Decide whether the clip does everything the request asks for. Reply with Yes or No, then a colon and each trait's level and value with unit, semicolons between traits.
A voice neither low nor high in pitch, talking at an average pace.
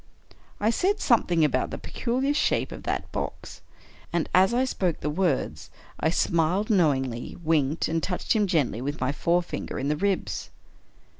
Yes: medium, 170 Hz; average, 170 wpm